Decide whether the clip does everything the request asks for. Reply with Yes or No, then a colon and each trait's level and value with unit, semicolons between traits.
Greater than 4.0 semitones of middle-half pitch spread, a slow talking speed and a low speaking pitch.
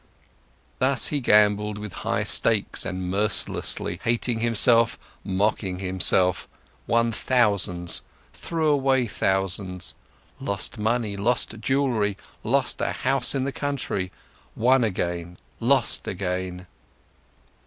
Yes: average, 4.7 semitones; slow, 105 wpm; low, 105 Hz